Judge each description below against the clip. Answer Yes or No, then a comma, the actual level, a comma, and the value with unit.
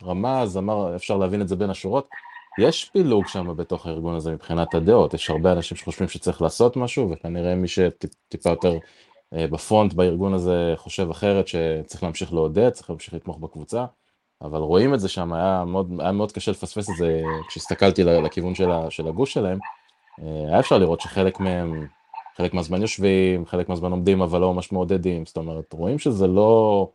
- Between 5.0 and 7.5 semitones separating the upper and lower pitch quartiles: No, average, 2.7 semitones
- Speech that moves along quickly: Yes, fast, 170 wpm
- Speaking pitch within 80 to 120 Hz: Yes, very low, 90 Hz